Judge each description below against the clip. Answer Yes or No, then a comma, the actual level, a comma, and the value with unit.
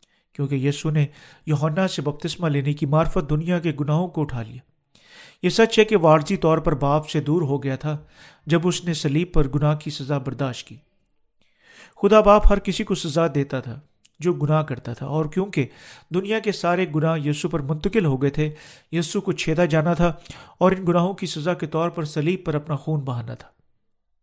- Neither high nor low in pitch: Yes, medium, 160 Hz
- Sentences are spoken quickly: Yes, fast, 200 wpm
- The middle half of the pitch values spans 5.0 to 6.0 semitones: No, average, 3.2 semitones